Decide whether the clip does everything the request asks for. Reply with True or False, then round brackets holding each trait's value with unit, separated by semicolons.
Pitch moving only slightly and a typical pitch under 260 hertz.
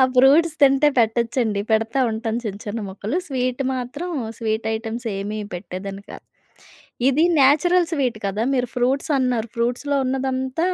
False (3.6 semitones; 245 Hz)